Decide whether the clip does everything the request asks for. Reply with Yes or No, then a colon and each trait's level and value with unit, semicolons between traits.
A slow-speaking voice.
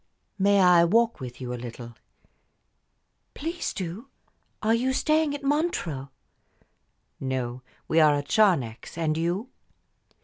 Yes: slow, 125 wpm